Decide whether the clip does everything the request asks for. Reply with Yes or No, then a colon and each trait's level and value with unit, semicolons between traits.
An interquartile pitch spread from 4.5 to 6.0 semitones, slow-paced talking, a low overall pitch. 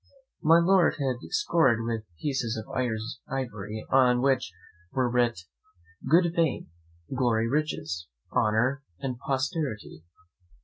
No: average, 4.0 semitones; slow, 105 wpm; low, 125 Hz